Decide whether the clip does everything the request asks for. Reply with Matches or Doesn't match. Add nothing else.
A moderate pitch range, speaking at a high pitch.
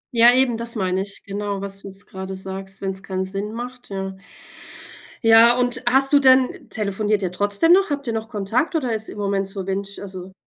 Matches